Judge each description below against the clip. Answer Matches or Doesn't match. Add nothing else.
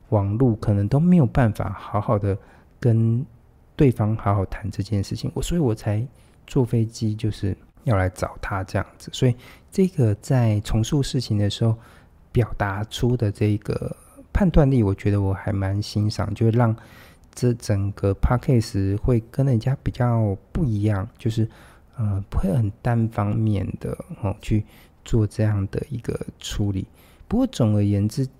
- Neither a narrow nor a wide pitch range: Matches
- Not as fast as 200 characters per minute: Doesn't match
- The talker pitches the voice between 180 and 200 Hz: Doesn't match